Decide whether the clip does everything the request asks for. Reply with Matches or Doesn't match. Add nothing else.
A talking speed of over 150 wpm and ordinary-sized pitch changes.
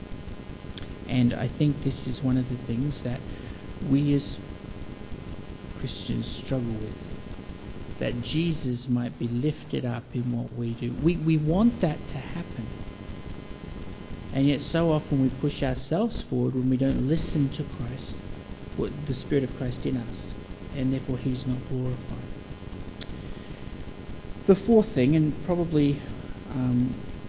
Doesn't match